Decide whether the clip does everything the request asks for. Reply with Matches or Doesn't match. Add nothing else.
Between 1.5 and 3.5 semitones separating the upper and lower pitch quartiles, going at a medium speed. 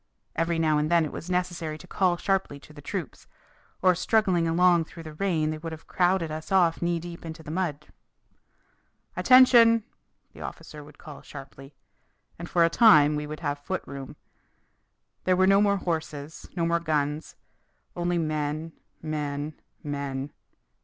Matches